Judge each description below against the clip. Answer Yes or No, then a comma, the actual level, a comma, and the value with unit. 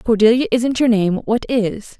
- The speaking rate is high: Yes, fast, 210 wpm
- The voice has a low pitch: No, high, 230 Hz